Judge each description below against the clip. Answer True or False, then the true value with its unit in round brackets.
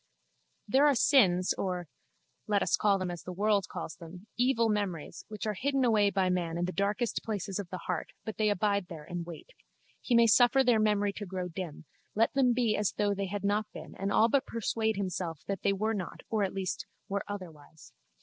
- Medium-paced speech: False (215 wpm)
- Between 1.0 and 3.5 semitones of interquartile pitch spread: True (3.2 semitones)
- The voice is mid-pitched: False (200 Hz)